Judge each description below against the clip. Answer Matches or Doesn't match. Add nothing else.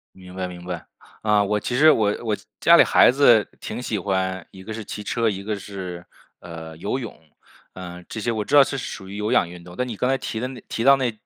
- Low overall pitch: Matches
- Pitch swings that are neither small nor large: Matches